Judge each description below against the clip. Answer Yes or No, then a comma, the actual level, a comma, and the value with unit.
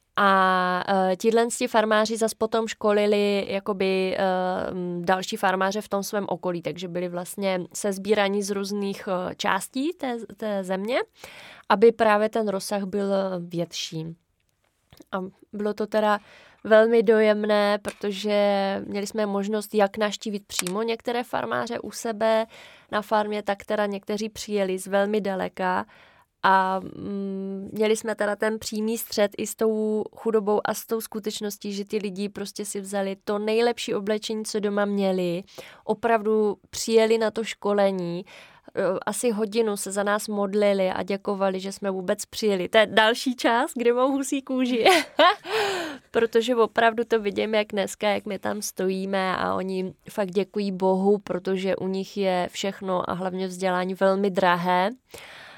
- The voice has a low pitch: No, high, 205 Hz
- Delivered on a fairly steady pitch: Yes, narrow, 2.2 semitones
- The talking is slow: No, average, 145 wpm